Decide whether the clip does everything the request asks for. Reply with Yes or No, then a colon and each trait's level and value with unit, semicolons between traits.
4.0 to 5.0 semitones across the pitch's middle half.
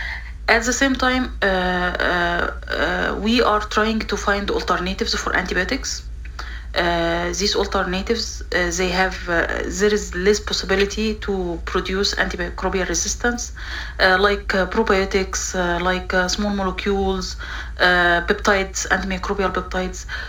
No: narrow, 2.4 semitones